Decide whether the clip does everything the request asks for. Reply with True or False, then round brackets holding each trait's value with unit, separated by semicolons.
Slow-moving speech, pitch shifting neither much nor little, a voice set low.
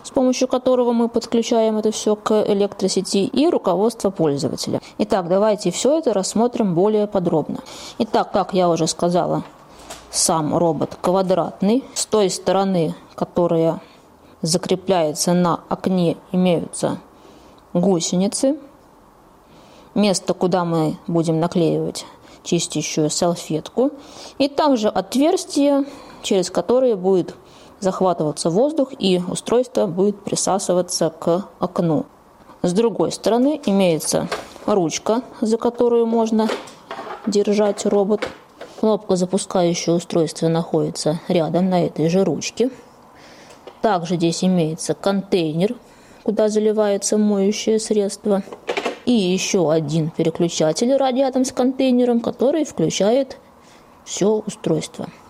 False (105 wpm; 4.9 semitones; 195 Hz)